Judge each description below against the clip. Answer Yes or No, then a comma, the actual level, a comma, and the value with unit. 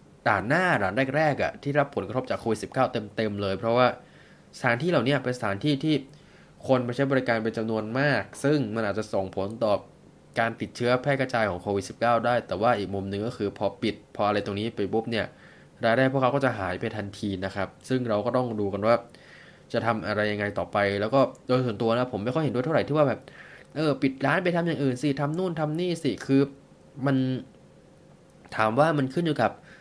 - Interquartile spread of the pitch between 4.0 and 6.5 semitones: Yes, average, 4.7 semitones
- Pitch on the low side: Yes, low, 120 Hz